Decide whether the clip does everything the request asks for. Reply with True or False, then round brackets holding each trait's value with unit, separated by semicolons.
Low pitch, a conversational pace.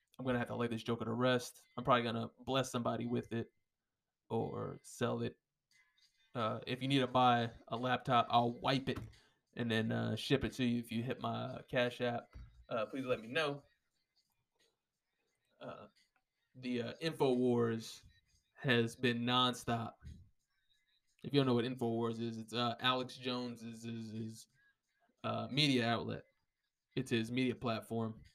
True (120 Hz; 160 wpm)